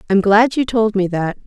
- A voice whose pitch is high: Yes, high, 210 Hz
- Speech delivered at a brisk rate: Yes, fast, 245 wpm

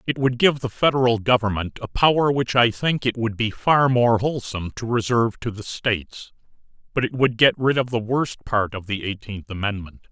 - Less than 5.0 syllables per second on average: No, 5.3 syllables/s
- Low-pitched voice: Yes, low, 120 Hz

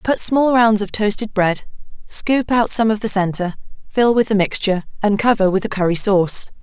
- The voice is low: No, high, 210 Hz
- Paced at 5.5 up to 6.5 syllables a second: No, 5.1 syllables/s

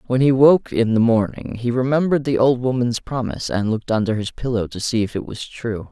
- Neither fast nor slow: No, fast, 235 wpm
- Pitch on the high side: No, low, 115 Hz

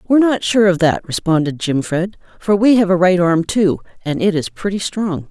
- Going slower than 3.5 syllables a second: No, 5.3 syllables/s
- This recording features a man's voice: No, female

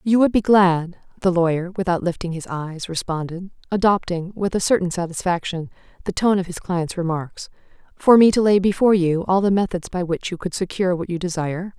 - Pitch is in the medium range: Yes, medium, 180 Hz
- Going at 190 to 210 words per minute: Yes, average, 200 wpm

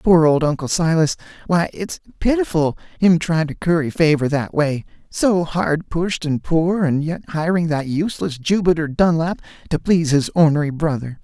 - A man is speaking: Yes, male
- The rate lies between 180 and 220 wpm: No, average, 155 wpm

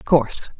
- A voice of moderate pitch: No, low, 125 Hz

